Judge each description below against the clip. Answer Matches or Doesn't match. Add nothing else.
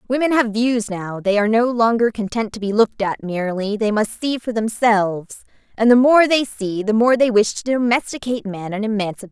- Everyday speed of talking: Doesn't match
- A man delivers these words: Doesn't match